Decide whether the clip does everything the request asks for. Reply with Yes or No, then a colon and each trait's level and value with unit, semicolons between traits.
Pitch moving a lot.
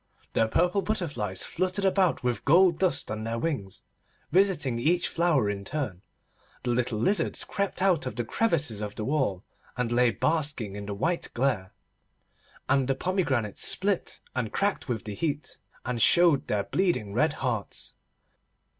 Yes: wide, 7.9 semitones